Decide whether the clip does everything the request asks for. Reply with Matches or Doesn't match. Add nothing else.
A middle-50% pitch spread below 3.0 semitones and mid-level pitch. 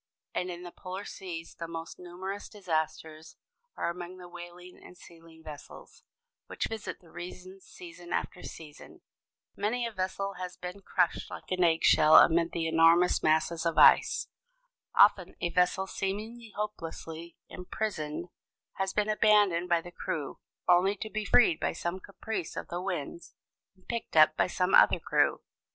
Matches